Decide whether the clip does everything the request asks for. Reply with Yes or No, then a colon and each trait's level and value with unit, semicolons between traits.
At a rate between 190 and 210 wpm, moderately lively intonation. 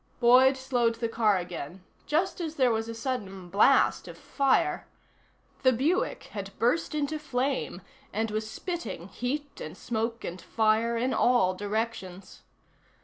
No: average, 145 wpm; average, 4.2 semitones